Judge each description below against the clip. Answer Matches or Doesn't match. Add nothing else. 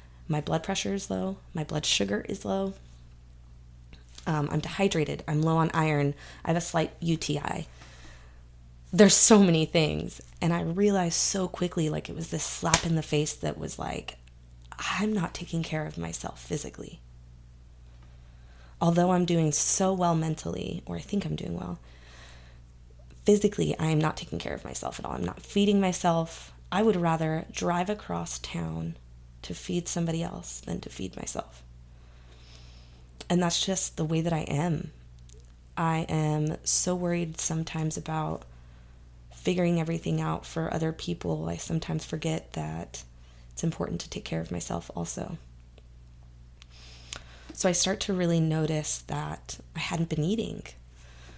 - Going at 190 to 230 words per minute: Doesn't match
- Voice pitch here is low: Matches